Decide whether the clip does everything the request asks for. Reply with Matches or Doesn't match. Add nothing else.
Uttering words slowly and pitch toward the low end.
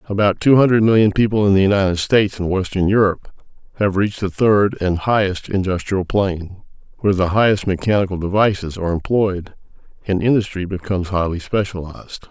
Doesn't match